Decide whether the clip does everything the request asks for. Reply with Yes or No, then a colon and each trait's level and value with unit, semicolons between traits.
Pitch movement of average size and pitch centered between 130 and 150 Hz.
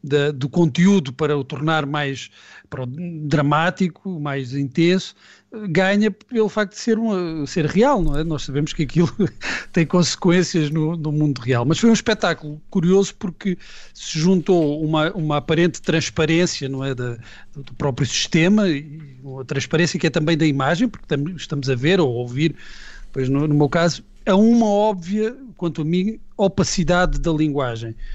No: average, 4.2 semitones; medium, 160 Hz